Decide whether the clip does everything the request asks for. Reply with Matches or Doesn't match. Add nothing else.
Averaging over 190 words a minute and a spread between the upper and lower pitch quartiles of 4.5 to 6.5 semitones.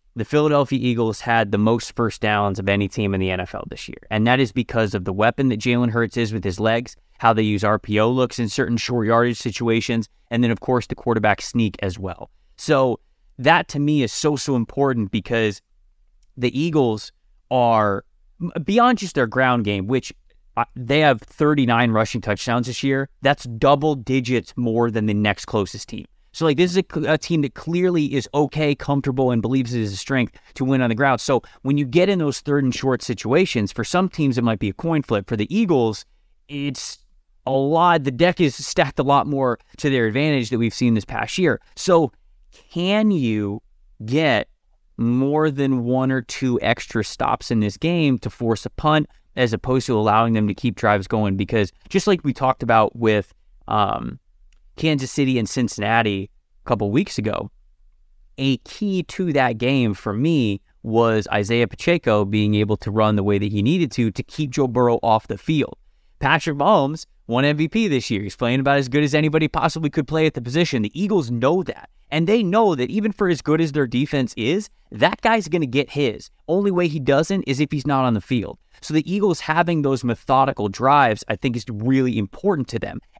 Matches